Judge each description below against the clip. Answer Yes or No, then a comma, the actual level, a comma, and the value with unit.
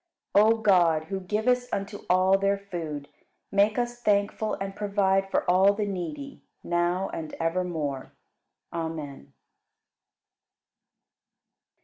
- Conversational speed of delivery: No, slow, 110 wpm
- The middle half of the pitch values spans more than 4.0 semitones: No, average, 3.1 semitones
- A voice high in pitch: Yes, high, 195 Hz